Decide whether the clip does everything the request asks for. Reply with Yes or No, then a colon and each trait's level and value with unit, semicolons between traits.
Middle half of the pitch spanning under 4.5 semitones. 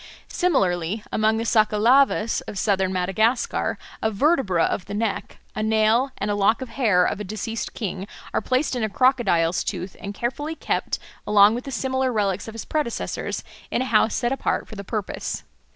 Yes: average, 3.6 semitones